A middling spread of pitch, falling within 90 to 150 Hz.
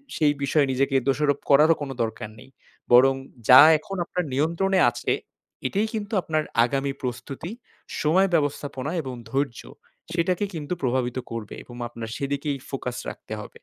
Yes: average, 3.6 semitones; medium, 140 Hz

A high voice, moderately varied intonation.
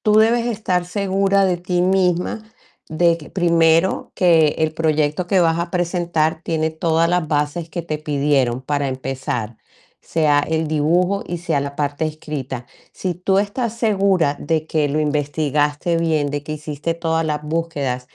No: medium, 160 Hz; average, 3.2 semitones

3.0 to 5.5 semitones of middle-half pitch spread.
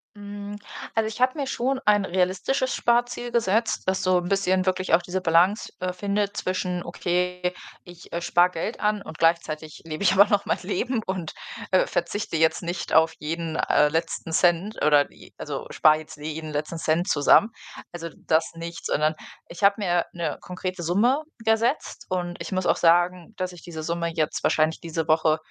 Yes: average, 3.4 semitones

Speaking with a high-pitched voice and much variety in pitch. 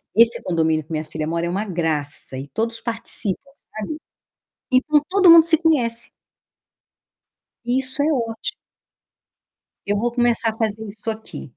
Yes: high, 225 Hz; wide, 6.7 semitones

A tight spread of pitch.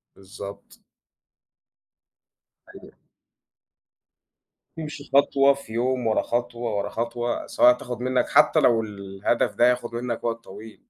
Yes: narrow, 2.1 semitones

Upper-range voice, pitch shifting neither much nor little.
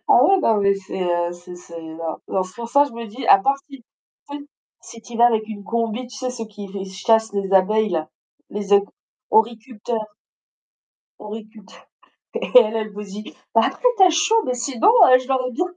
Yes: high, 220 Hz; average, 3.7 semitones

